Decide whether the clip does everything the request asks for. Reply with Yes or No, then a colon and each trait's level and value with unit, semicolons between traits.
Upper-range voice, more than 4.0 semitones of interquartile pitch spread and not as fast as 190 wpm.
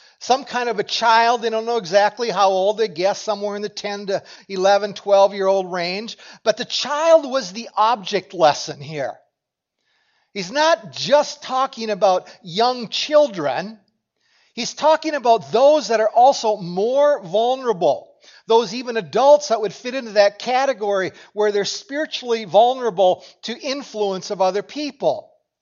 Yes: high, 225 Hz; average, 4.9 semitones; average, 150 wpm